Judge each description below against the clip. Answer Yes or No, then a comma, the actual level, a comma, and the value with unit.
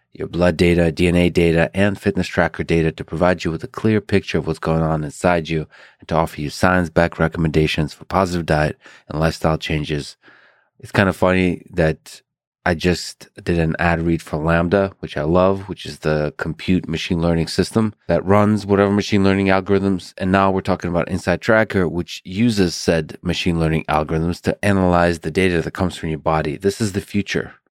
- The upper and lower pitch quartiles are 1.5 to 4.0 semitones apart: Yes, average, 2.9 semitones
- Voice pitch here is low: Yes, very low, 85 Hz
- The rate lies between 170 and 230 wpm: Yes, average, 195 wpm